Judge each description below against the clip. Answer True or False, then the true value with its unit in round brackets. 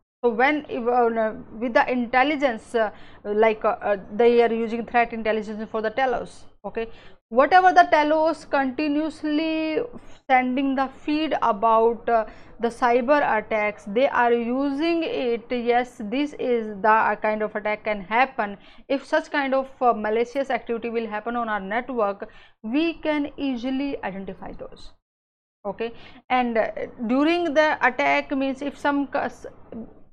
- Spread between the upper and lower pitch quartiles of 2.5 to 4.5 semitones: True (4.0 semitones)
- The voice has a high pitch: True (240 Hz)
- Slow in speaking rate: True (125 wpm)